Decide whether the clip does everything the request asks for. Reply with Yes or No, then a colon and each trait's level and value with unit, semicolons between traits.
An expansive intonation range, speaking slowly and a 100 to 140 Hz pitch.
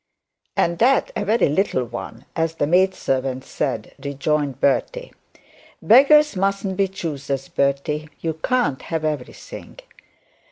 No: wide, 6.0 semitones; slow, 125 wpm; medium, 160 Hz